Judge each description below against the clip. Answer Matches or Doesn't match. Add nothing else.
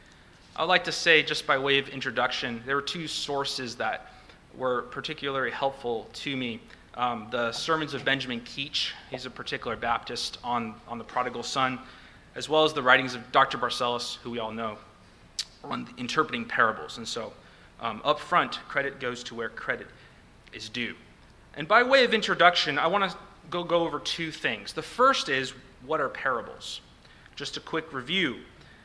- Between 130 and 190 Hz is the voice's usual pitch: Matches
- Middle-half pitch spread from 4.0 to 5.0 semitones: Matches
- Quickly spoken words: Doesn't match